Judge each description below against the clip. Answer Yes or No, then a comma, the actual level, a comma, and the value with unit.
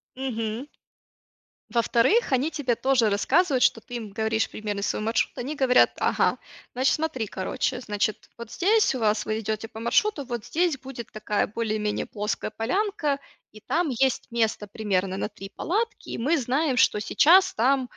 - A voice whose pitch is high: Yes, high, 235 Hz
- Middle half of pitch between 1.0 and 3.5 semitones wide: No, average, 4.3 semitones